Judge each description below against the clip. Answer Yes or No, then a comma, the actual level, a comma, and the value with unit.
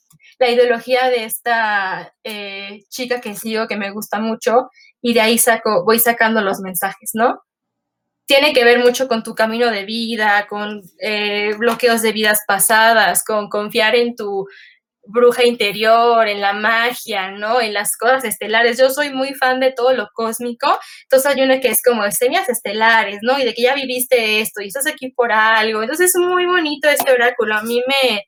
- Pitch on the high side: Yes, high, 230 Hz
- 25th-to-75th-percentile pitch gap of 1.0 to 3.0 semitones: Yes, average, 2.7 semitones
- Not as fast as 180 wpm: No, average, 185 wpm